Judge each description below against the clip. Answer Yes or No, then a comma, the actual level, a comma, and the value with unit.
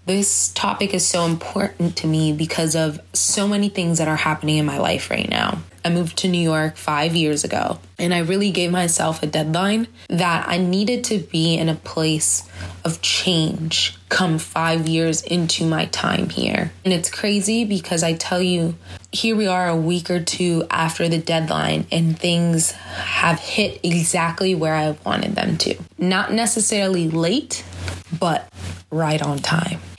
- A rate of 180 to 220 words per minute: No, average, 170 wpm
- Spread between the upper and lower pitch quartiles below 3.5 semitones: Yes, narrow, 2.5 semitones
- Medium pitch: Yes, medium, 165 Hz